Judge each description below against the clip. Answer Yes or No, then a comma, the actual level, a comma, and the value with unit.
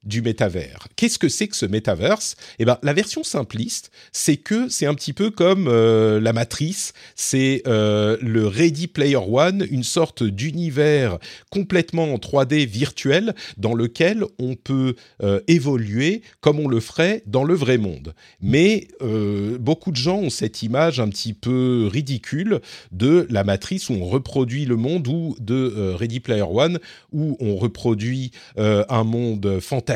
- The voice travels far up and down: Yes, wide, 6.3 semitones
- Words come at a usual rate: Yes, average, 165 wpm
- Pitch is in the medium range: No, low, 130 Hz